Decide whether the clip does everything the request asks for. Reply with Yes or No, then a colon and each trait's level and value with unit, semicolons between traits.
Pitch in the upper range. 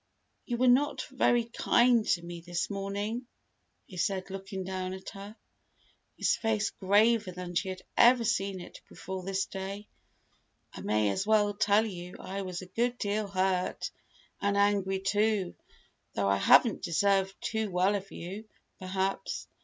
Yes: high, 195 Hz